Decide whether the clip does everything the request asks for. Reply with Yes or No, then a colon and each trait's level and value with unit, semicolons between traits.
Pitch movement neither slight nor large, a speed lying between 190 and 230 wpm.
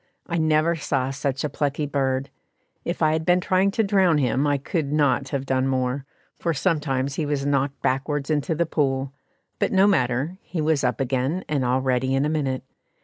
Yes: average, 3.1 semitones; average, 200 wpm